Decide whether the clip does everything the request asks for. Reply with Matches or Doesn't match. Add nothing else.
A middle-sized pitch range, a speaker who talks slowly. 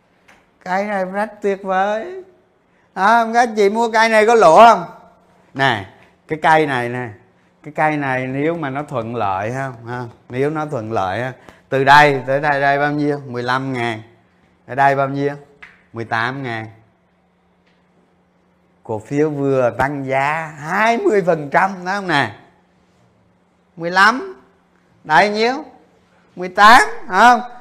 Doesn't match